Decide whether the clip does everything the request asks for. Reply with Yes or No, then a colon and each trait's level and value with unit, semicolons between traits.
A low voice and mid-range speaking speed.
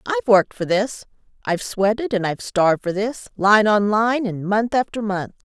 No: high, 205 Hz; average, 195 wpm